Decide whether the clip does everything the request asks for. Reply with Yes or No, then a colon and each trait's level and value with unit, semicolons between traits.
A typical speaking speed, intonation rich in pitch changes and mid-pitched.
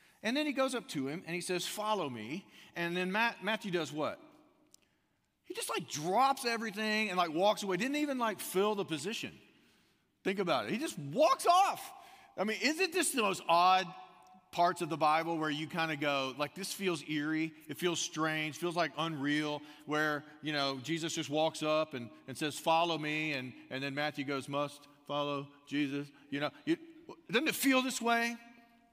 Yes: average, 195 wpm; wide, 7.5 semitones; medium, 175 Hz